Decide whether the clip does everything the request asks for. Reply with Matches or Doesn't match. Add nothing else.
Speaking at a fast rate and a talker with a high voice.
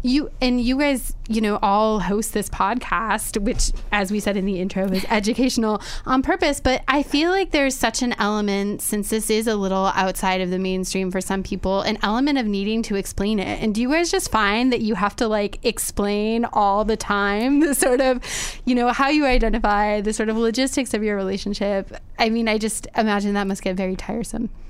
Matches